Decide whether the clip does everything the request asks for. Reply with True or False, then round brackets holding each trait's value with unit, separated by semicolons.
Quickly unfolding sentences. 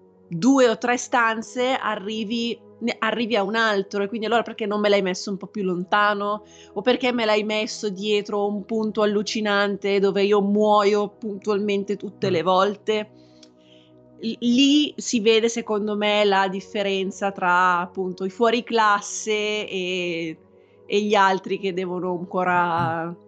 False (150 wpm)